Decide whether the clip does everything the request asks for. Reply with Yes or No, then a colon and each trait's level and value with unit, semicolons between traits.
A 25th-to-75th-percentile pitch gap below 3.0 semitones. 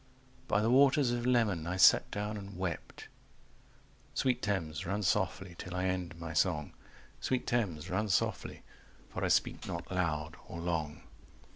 No: average, 3.8 semitones